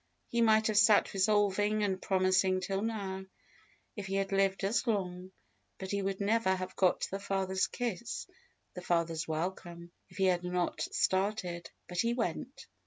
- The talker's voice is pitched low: No, high, 190 Hz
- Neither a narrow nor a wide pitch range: No, narrow, 2.1 semitones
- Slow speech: No, average, 165 wpm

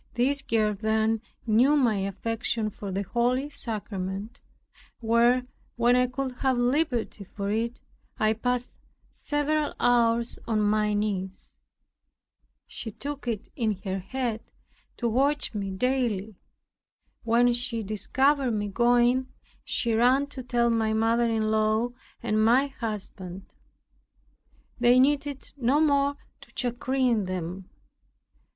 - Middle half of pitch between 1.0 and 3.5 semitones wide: Yes, average, 2.9 semitones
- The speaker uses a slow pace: Yes, slow, 120 wpm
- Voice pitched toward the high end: Yes, high, 235 Hz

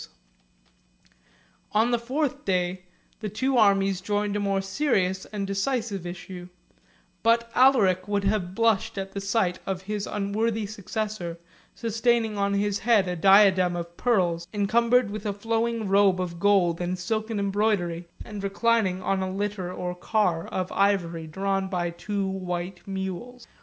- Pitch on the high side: Yes, high, 200 Hz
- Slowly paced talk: No, average, 150 wpm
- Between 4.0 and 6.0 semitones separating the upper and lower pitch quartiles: No, average, 2.9 semitones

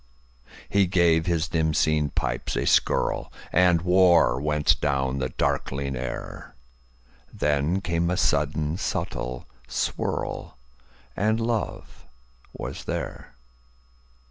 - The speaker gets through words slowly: Yes, slow, 90 wpm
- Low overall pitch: Yes, very low, 75 Hz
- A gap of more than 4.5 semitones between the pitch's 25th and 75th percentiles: Yes, average, 5.1 semitones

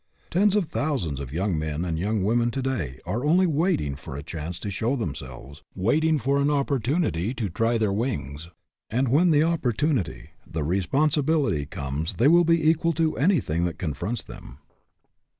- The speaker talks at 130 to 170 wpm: No, average, 180 wpm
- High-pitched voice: No, low, 115 Hz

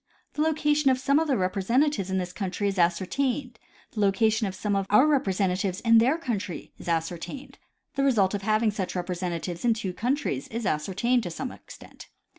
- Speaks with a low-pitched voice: No, high, 210 Hz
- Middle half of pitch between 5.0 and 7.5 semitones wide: Yes, wide, 5.5 semitones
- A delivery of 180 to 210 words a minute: Yes, average, 190 wpm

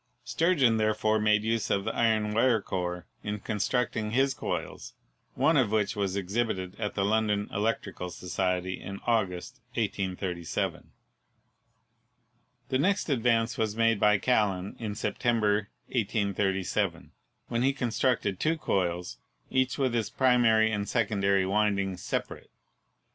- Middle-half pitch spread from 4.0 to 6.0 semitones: No, average, 3.1 semitones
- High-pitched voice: No, low, 105 Hz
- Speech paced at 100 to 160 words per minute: Yes, slow, 135 wpm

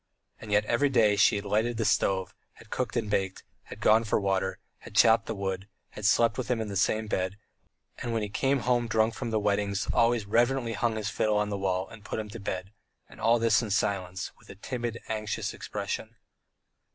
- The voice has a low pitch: Yes, low, 110 Hz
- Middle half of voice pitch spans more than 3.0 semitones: No, narrow, 2.6 semitones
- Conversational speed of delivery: No, fast, 220 wpm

